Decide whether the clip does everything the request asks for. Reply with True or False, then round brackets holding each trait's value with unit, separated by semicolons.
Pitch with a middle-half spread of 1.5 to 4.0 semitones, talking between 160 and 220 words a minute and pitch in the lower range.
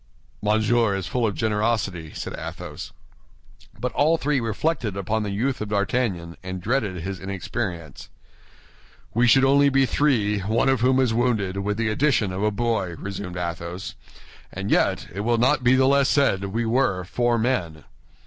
False (4.5 semitones; 170 wpm; 110 Hz)